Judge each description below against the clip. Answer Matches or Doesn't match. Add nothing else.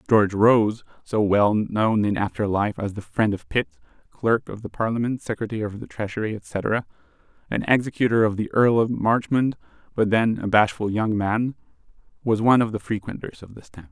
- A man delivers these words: Matches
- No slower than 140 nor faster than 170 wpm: Doesn't match